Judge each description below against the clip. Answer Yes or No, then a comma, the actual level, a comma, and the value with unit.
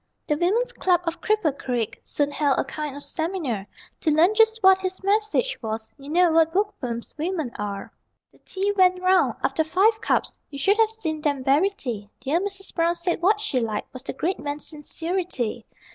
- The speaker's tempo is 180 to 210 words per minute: Yes, average, 190 wpm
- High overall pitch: Yes, very high, 330 Hz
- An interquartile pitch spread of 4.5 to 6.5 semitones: Yes, wide, 5.5 semitones